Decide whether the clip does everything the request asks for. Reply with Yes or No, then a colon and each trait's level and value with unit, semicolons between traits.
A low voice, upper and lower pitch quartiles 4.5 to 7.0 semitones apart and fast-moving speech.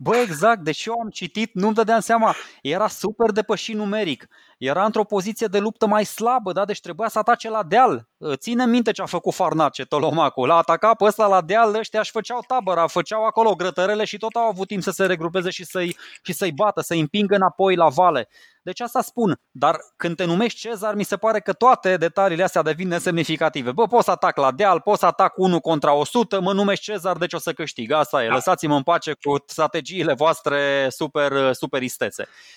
No: high, 190 Hz; average, 4.8 semitones; fast, 205 wpm